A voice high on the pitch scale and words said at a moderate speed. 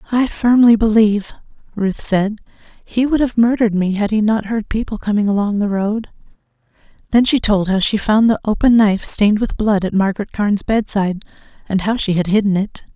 Yes: high, 210 Hz; average, 190 wpm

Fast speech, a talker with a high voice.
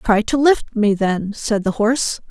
Yes: fast, 210 wpm; high, 220 Hz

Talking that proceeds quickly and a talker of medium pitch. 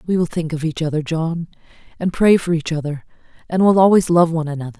Yes: fast, 225 wpm; medium, 165 Hz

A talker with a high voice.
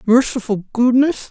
Yes: high, 240 Hz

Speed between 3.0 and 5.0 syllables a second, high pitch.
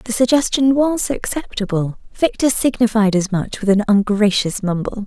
Yes: 4.8 syllables/s; high, 220 Hz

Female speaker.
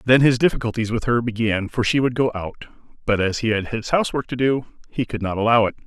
No: male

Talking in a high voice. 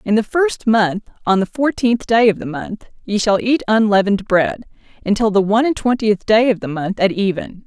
Yes: high, 210 Hz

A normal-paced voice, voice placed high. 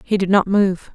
No: fast, 255 wpm; high, 195 Hz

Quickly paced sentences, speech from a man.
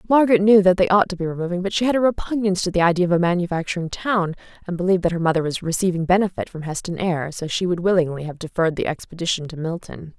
No: fast, 240 wpm; female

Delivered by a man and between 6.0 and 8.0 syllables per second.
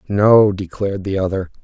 No: male; 5.2 syllables/s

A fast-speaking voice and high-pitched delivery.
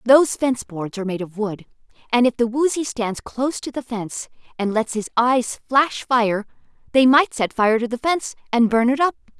Yes: fast, 210 wpm; high, 240 Hz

